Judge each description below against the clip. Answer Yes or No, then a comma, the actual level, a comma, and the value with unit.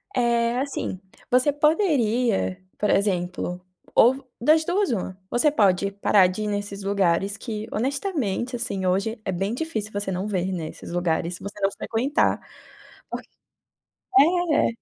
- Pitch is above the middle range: Yes, high, 210 Hz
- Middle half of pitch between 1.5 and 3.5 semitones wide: No, average, 5.2 semitones